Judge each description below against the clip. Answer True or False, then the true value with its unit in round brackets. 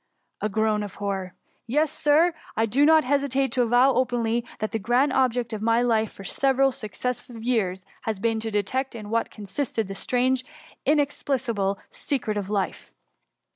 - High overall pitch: True (235 Hz)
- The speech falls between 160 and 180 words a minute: True (175 wpm)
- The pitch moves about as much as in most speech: True (3.7 semitones)